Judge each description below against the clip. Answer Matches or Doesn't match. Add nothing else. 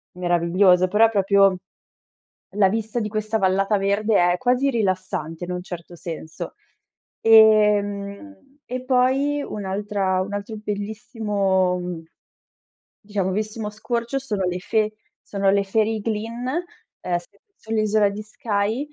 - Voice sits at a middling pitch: Doesn't match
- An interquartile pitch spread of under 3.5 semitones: Matches